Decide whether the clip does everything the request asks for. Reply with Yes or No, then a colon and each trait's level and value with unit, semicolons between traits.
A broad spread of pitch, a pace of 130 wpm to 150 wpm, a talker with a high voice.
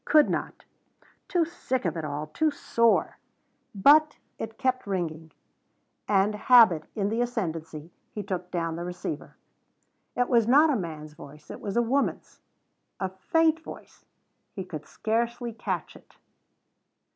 Yes: wide, 6.8 semitones; average, 145 wpm; high, 205 Hz